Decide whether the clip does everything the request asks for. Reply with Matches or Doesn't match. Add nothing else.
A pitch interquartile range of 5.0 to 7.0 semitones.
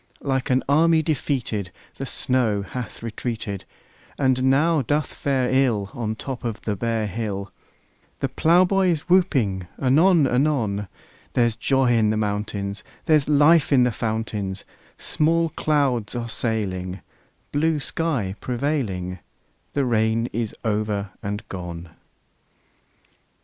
Matches